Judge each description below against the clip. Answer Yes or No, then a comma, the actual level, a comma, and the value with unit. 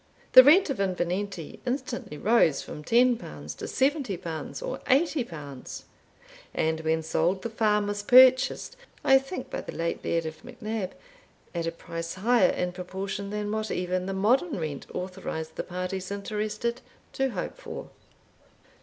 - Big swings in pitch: Yes, wide, 6.0 semitones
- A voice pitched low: No, high, 200 Hz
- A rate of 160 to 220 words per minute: No, average, 145 wpm